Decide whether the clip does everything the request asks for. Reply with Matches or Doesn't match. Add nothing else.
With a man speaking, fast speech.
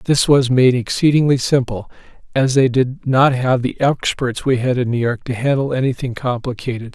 Doesn't match